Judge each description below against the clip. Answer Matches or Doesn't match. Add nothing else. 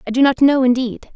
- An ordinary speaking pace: Doesn't match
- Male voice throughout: Doesn't match